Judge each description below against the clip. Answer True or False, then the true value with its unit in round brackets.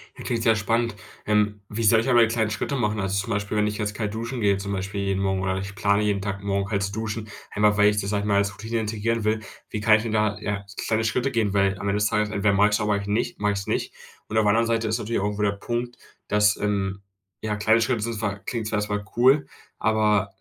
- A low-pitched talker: True (105 Hz)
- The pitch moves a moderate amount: False (1.7 semitones)